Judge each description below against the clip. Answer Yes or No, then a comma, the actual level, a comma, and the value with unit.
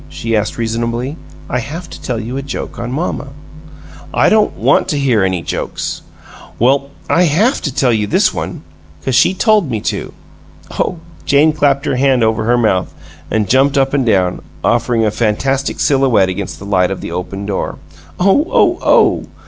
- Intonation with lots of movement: No, average, 4.6 semitones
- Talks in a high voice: No, low, 125 Hz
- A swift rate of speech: No, average, 180 wpm